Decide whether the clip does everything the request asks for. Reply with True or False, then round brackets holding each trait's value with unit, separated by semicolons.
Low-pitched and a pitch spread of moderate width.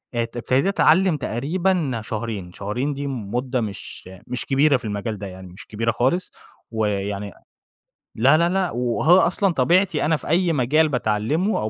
False (125 Hz; 6.8 semitones)